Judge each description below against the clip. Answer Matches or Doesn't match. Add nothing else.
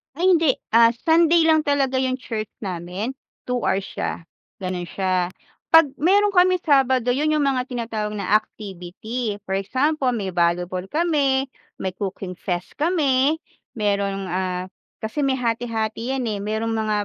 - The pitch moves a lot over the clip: Matches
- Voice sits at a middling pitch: Doesn't match